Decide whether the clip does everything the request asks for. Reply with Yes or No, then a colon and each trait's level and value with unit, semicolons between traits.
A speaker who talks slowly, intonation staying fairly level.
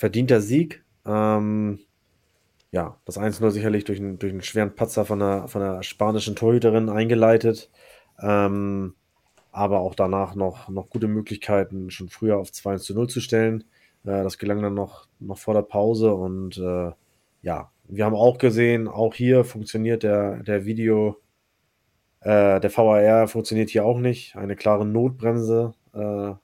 No: average, 150 wpm; narrow, 2.2 semitones